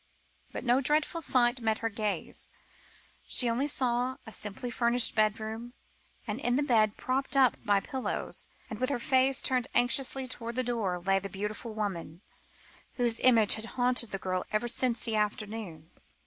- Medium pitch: No, high, 235 Hz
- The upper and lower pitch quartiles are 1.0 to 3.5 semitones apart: Yes, average, 3.2 semitones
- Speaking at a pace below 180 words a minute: Yes, average, 165 wpm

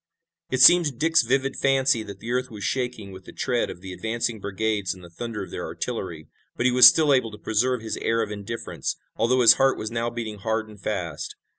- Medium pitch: No, low, 115 Hz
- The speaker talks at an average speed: No, fast, 230 wpm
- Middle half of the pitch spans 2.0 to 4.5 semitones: Yes, average, 3.5 semitones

